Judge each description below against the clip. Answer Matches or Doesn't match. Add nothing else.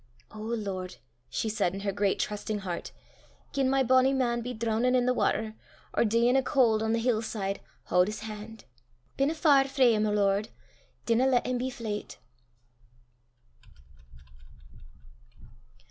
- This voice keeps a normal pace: Matches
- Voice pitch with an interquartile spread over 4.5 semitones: Doesn't match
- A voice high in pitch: Matches